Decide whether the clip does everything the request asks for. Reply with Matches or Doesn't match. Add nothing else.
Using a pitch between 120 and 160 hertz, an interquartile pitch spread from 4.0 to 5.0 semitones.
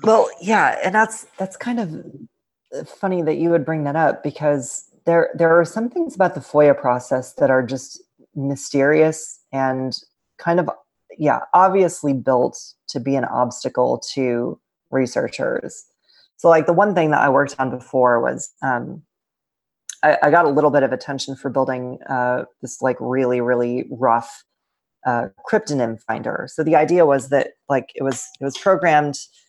Matches